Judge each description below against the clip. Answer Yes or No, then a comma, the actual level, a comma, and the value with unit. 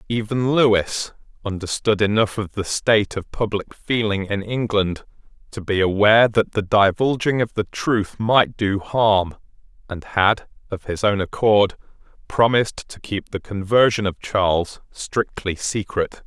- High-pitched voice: No, low, 105 Hz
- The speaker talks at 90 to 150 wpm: Yes, average, 145 wpm